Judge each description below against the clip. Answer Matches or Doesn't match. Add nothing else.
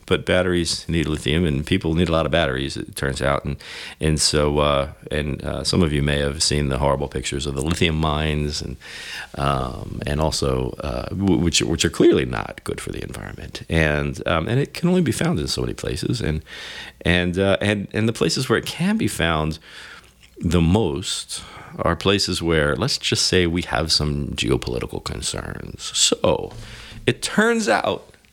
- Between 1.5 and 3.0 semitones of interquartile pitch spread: Doesn't match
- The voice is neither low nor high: Doesn't match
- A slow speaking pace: Doesn't match